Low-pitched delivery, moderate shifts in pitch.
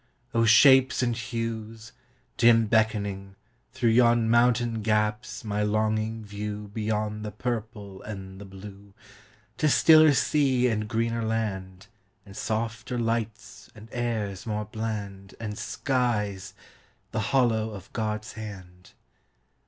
No: low, 110 Hz; narrow, 1.9 semitones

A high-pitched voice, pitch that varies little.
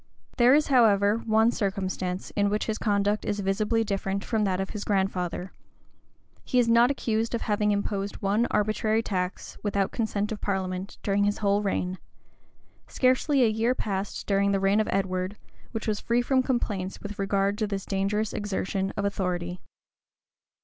Yes: high, 205 Hz; narrow, 2.0 semitones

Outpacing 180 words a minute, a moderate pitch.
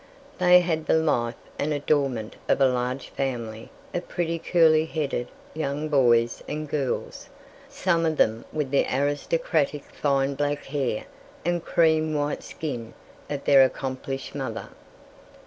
No: slow, 135 wpm; medium, 145 Hz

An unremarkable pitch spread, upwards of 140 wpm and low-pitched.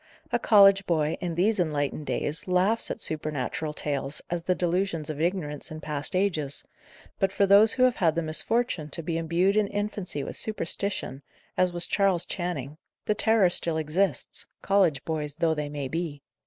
No: average, 4.5 semitones; average, 175 wpm; medium, 170 Hz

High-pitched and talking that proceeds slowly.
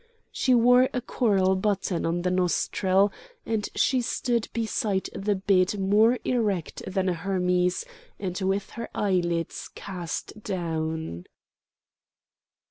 Yes: high, 195 Hz; slow, 120 wpm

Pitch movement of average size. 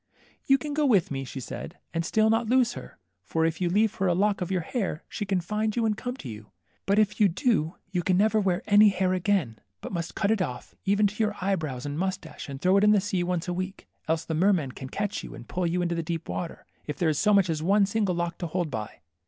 Yes: average, 4.0 semitones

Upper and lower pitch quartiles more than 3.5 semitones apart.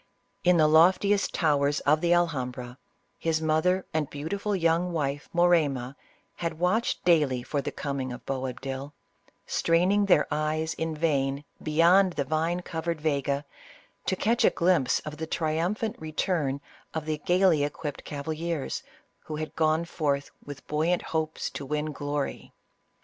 No: average, 3.0 semitones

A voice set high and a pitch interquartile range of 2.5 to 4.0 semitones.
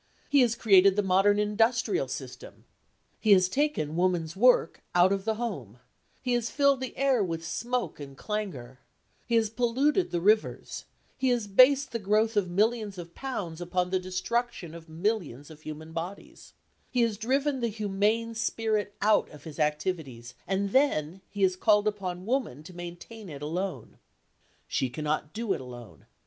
No: high, 200 Hz; wide, 5.4 semitones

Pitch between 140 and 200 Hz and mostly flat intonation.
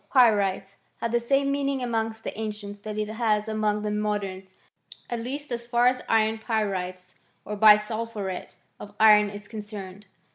No: high, 215 Hz; narrow, 2.2 semitones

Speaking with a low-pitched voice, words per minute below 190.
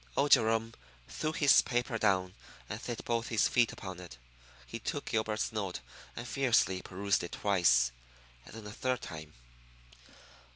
Yes: low, 110 Hz; average, 155 wpm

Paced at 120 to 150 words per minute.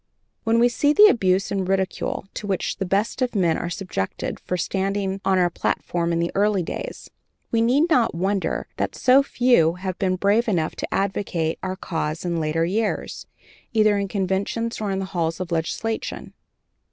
No: average, 180 wpm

